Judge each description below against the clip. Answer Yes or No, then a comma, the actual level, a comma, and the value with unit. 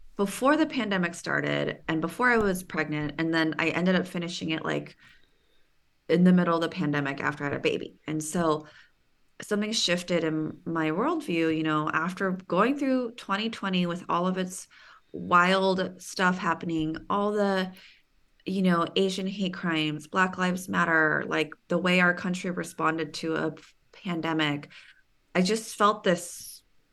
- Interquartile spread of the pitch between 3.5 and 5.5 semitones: No, average, 3.1 semitones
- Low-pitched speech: No, medium, 175 Hz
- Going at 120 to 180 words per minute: Yes, average, 160 wpm